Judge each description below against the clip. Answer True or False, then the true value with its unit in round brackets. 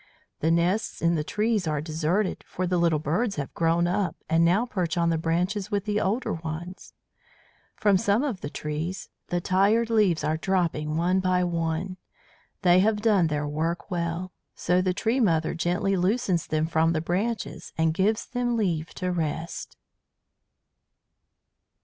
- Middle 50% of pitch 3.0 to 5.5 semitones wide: True (3.6 semitones)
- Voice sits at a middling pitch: True (175 Hz)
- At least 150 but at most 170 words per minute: True (160 wpm)